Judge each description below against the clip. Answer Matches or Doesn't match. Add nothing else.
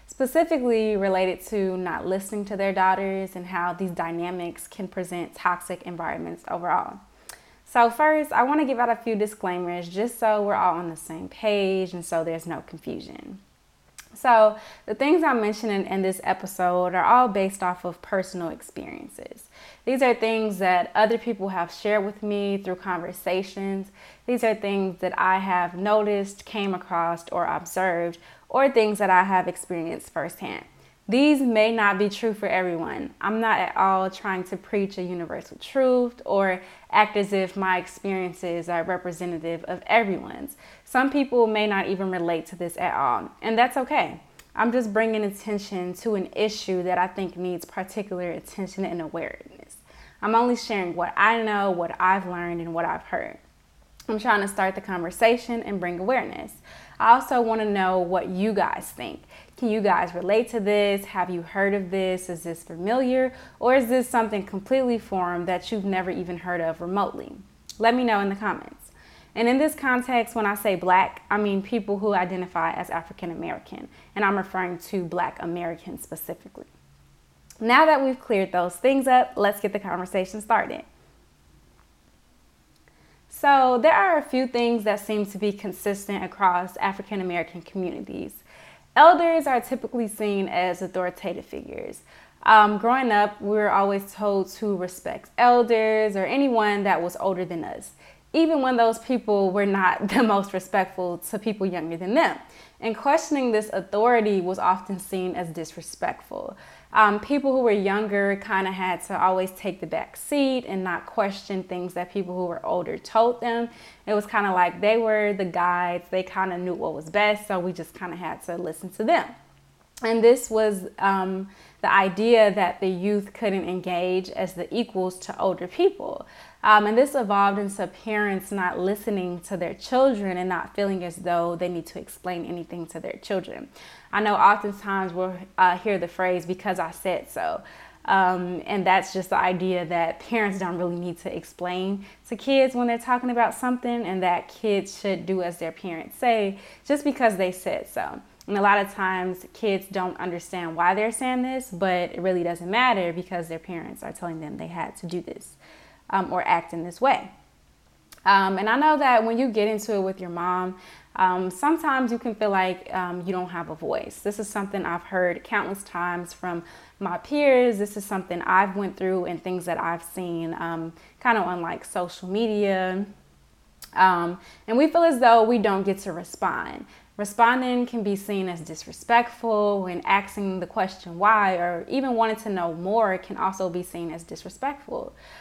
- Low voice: Doesn't match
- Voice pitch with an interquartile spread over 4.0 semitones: Doesn't match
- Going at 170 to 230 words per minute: Matches